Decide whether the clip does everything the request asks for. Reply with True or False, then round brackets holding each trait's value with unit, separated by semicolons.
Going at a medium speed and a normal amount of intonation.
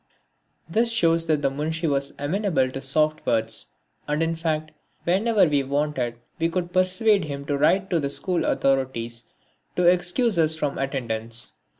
True (160 wpm; 4.4 semitones)